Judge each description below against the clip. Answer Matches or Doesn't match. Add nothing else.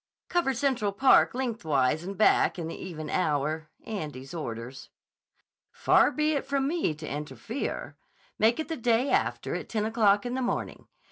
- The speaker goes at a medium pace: Matches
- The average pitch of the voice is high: Matches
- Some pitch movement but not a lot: Doesn't match